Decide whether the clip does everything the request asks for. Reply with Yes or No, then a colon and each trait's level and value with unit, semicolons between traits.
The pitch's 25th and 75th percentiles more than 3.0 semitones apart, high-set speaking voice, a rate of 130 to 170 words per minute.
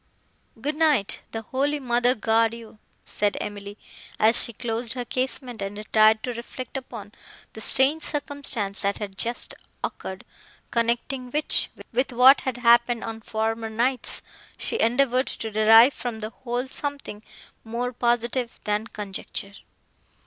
No: average, 2.7 semitones; high, 235 Hz; average, 140 wpm